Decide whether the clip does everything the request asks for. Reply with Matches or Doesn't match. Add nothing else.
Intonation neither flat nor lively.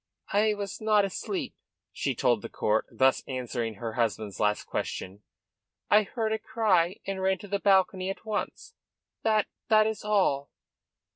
Doesn't match